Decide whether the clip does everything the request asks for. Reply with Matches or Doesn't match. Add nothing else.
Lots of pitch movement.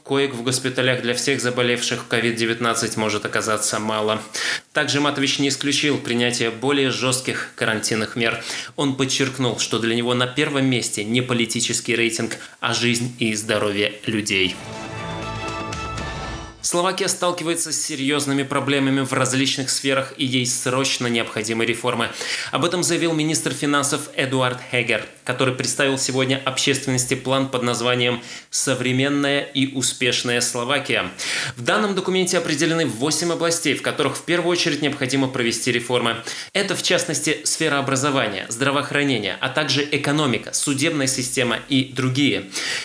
Doesn't match